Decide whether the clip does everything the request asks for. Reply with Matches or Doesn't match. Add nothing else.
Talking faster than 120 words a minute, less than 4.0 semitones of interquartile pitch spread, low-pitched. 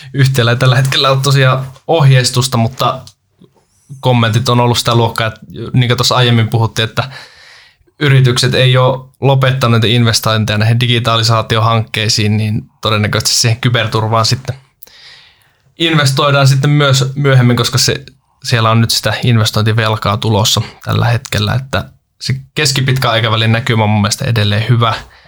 Matches